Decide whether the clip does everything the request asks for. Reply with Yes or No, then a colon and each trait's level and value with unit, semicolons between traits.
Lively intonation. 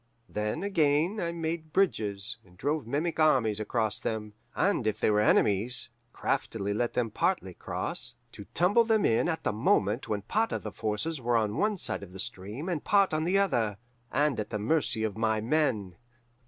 Yes: wide, 7.4 semitones